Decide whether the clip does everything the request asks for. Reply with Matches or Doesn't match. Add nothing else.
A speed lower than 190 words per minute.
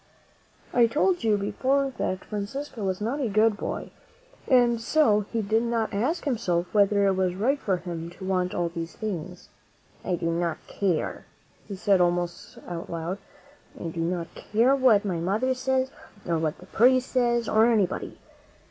Matches